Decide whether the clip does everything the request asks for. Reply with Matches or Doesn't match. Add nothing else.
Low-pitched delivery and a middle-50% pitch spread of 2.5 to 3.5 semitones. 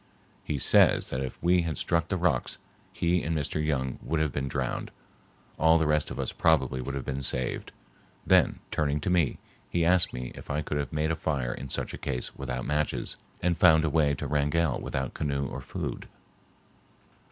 Matches